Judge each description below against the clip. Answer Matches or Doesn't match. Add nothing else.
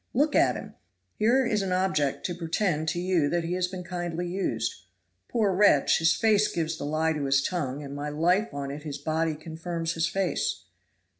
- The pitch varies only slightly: Doesn't match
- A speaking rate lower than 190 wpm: Doesn't match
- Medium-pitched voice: Matches